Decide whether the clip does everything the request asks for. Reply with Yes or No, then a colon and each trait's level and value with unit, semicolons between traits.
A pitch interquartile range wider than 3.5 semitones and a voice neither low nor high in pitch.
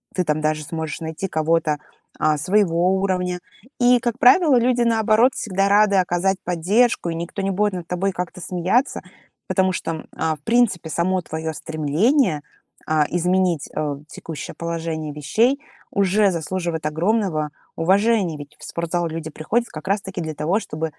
Yes: average, 4.1 semitones; medium, 180 Hz